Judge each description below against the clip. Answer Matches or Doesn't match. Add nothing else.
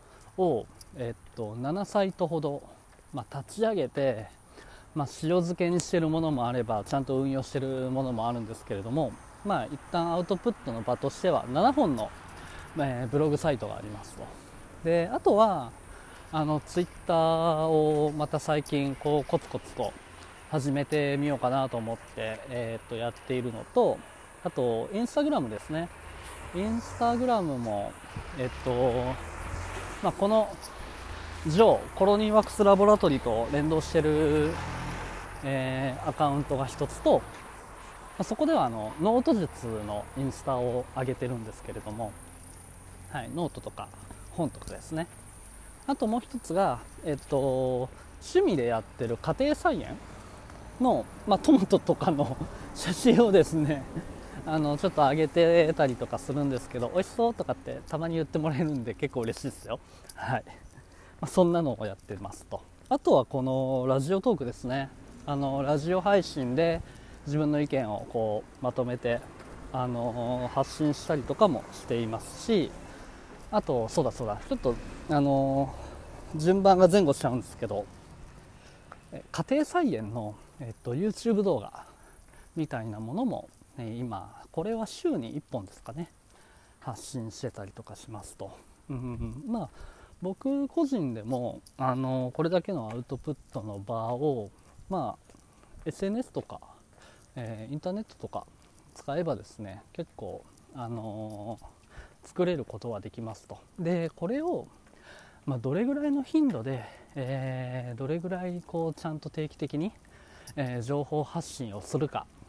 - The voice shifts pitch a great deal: Matches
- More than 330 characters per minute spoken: Doesn't match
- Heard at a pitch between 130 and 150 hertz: Matches